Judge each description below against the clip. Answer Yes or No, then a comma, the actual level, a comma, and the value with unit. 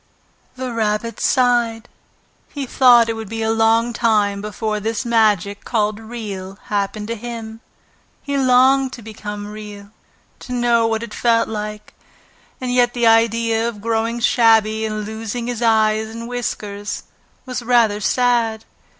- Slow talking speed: No, average, 145 wpm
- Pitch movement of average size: No, narrow, 2.0 semitones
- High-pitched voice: Yes, high, 225 Hz